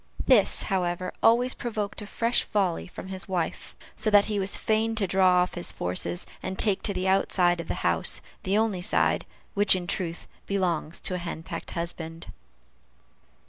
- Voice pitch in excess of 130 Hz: Yes, high, 190 Hz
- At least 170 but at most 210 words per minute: Yes, average, 175 wpm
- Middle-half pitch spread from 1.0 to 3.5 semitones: Yes, average, 2.9 semitones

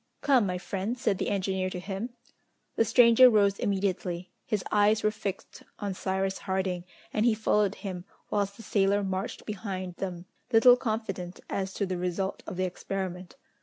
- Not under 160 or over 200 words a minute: Yes, average, 165 wpm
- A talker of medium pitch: No, high, 195 Hz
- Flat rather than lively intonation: Yes, narrow, 2.3 semitones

